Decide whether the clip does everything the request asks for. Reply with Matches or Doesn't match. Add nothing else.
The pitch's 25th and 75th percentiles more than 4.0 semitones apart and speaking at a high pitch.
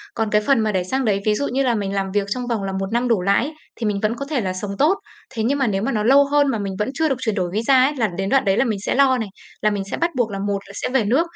Matches